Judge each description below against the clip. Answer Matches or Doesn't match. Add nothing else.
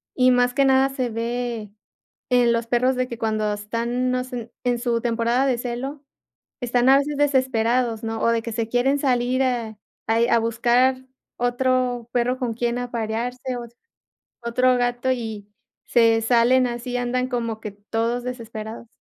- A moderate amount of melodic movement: Doesn't match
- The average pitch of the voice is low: Doesn't match